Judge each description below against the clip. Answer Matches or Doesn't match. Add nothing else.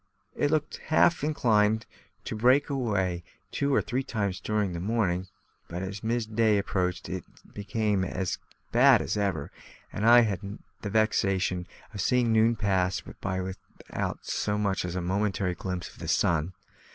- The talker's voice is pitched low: Matches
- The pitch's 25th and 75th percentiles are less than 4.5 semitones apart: Matches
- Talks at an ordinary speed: Matches